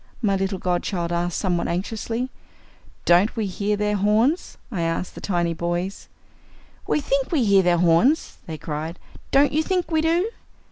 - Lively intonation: Yes, wide, 6.5 semitones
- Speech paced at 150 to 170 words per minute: Yes, average, 160 wpm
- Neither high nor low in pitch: No, high, 195 Hz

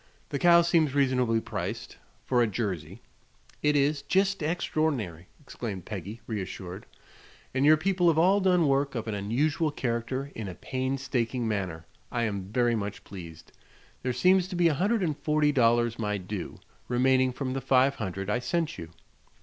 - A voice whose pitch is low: Yes, low, 130 Hz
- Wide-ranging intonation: Yes, wide, 6.1 semitones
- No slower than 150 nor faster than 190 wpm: Yes, average, 165 wpm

